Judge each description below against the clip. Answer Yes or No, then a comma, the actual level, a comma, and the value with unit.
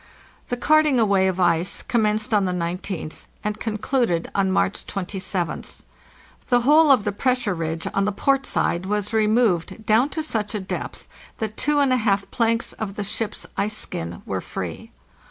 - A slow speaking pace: No, average, 175 wpm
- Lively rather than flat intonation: No, average, 4.0 semitones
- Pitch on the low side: No, high, 210 Hz